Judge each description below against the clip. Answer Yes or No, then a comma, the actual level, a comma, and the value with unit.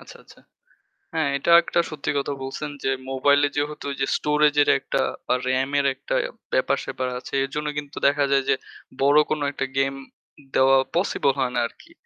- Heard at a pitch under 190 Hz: Yes, medium, 140 Hz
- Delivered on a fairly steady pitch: Yes, narrow, 1.7 semitones